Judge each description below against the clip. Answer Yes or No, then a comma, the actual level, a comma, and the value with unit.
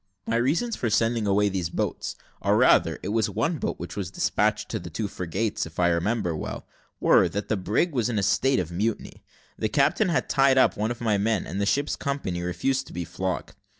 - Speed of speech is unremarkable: No, fast, 220 wpm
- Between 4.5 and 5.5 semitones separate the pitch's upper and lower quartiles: Yes, average, 4.9 semitones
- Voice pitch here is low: Yes, low, 105 Hz